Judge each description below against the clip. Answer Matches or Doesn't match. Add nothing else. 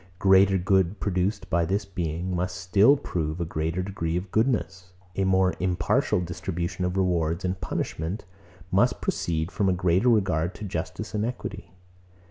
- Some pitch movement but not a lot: Doesn't match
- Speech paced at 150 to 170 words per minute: Matches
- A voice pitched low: Matches